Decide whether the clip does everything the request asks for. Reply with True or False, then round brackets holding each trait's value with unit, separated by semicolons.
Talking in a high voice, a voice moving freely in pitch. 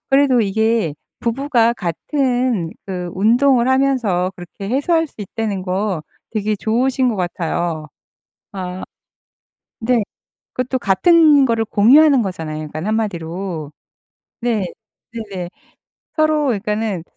True (220 Hz; 5.7 semitones)